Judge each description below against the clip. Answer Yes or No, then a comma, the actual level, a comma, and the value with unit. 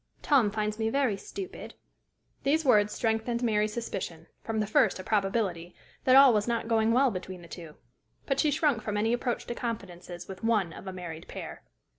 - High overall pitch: Yes, high, 220 Hz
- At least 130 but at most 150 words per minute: No, average, 190 wpm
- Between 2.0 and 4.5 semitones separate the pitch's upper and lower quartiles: Yes, average, 4.0 semitones